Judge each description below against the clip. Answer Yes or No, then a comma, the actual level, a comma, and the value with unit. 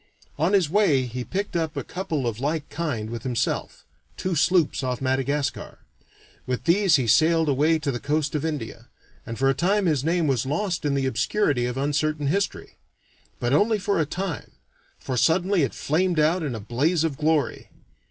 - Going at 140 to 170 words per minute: No, average, 185 wpm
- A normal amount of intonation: Yes, average, 4.3 semitones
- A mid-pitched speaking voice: Yes, medium, 150 Hz